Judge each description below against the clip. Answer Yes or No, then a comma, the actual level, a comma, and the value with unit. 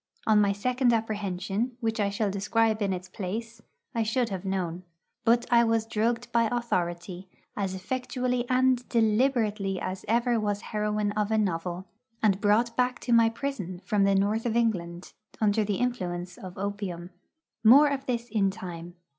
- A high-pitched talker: Yes, high, 215 Hz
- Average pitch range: Yes, average, 3.5 semitones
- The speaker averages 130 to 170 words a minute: Yes, average, 165 wpm